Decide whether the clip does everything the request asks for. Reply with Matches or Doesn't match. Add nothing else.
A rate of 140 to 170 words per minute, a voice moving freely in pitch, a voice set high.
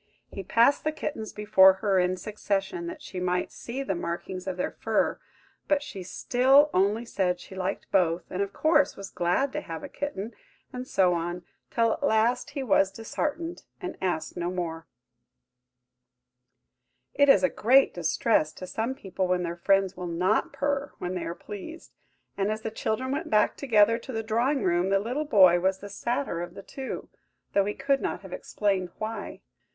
Doesn't match